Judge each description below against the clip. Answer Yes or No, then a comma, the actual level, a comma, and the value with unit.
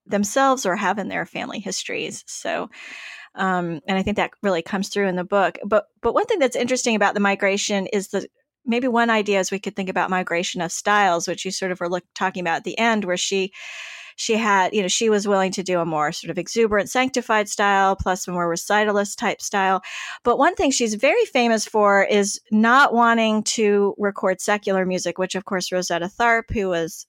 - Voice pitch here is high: Yes, high, 200 Hz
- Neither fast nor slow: No, fast, 215 wpm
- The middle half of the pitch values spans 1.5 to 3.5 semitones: Yes, average, 3.0 semitones